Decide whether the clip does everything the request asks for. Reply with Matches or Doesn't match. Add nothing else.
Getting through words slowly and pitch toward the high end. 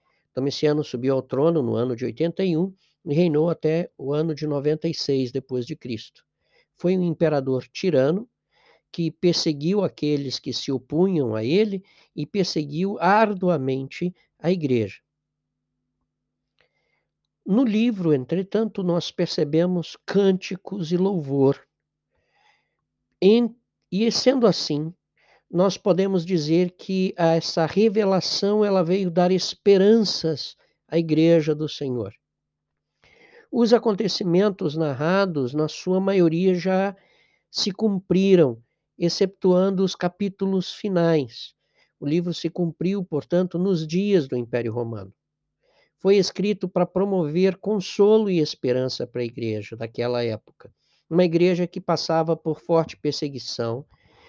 Doesn't match